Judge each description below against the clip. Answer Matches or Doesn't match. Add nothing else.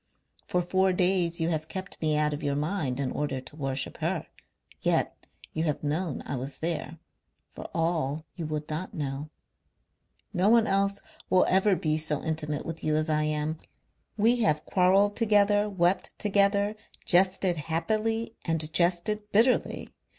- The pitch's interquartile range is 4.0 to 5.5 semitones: Matches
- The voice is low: Doesn't match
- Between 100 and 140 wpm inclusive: Doesn't match